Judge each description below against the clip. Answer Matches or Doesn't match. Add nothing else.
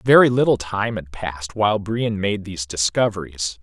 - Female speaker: Doesn't match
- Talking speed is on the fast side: Doesn't match